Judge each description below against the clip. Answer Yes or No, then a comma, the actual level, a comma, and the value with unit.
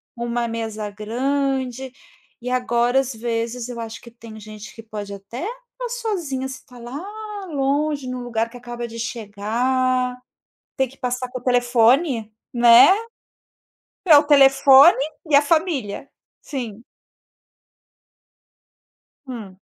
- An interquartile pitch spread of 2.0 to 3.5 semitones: Yes, average, 2.8 semitones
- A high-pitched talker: Yes, high, 245 Hz